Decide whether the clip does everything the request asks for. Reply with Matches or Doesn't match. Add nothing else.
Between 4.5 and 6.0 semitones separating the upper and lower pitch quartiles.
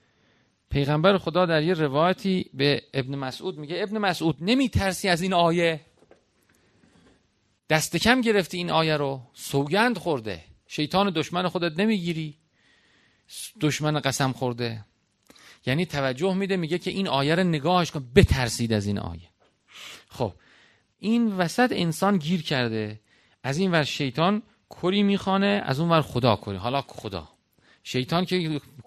Matches